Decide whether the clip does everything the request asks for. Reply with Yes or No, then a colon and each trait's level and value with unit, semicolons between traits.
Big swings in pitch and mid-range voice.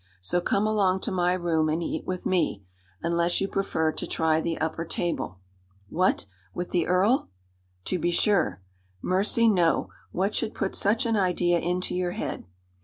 No: narrow, 2.6 semitones; medium, 180 Hz